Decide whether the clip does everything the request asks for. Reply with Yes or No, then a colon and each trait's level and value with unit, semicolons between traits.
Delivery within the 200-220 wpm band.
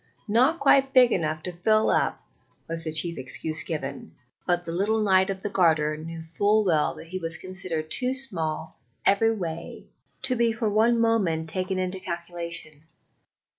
No: average, 170 wpm